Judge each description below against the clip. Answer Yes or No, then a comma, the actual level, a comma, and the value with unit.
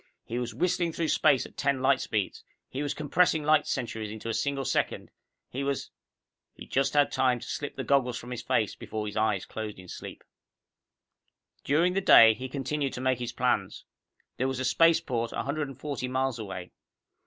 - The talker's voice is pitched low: Yes, low, 130 Hz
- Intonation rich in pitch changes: No, average, 3.7 semitones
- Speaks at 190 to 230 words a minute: Yes, average, 195 wpm